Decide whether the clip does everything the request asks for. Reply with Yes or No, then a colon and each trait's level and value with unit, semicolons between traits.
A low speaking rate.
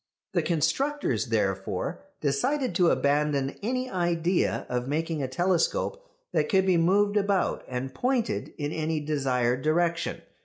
Yes: slow, 130 wpm